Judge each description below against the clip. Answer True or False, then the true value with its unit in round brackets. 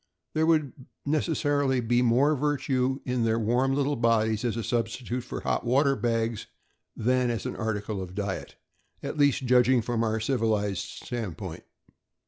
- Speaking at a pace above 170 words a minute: False (160 wpm)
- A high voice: False (120 Hz)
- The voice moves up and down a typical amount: True (3.1 semitones)